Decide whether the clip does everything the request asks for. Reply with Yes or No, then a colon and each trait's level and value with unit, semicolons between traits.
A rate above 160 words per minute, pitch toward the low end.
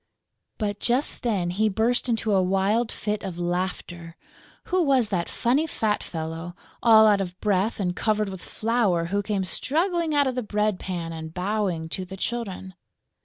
No: average, 170 wpm; high, 205 Hz